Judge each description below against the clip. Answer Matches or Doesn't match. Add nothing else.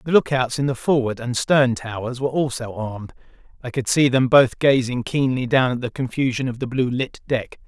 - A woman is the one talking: Doesn't match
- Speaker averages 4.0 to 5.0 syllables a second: Doesn't match